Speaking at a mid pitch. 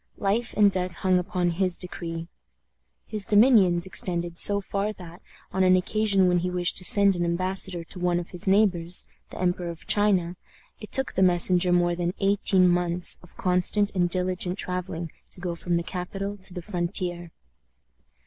Yes: medium, 180 Hz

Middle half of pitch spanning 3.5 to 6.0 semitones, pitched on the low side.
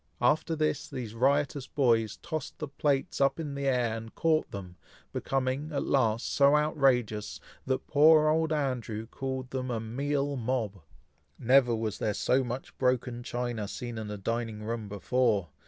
Yes: average, 3.8 semitones; low, 125 Hz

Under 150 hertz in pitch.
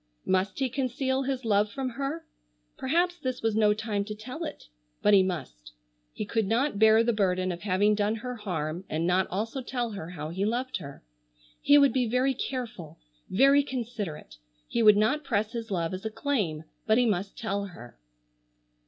No: high, 220 Hz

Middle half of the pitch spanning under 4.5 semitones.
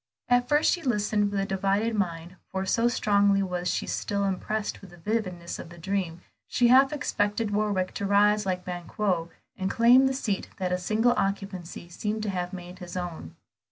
Yes: average, 2.9 semitones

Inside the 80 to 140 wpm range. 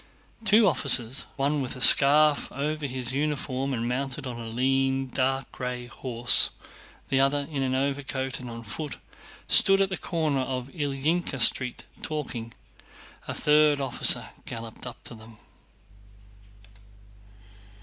Yes: slow, 135 wpm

